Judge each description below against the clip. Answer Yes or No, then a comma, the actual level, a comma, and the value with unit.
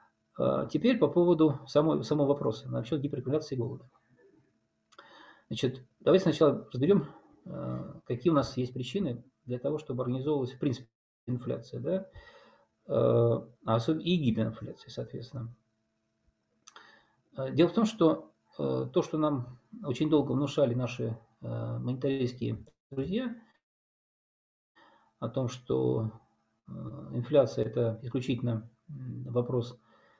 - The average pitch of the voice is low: Yes, low, 125 Hz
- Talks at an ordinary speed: No, slow, 100 wpm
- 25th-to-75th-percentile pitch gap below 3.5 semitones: No, average, 4.4 semitones